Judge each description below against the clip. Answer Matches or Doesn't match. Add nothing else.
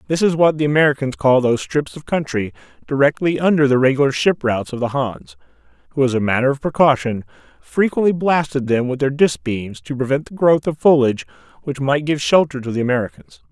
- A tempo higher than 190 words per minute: Matches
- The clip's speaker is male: Matches